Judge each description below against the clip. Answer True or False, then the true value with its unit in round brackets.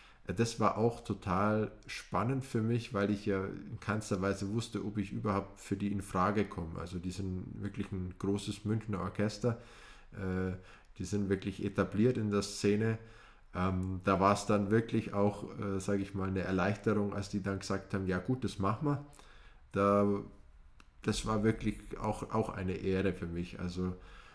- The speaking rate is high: False (165 wpm)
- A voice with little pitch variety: True (2.1 semitones)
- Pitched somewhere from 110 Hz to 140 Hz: False (100 Hz)